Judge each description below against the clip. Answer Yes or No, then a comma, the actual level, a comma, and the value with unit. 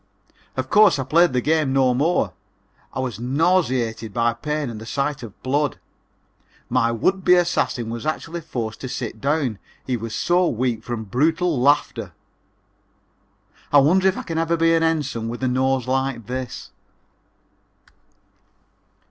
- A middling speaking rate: Yes, average, 155 wpm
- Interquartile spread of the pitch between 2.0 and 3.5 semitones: No, average, 5.2 semitones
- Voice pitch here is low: Yes, low, 130 Hz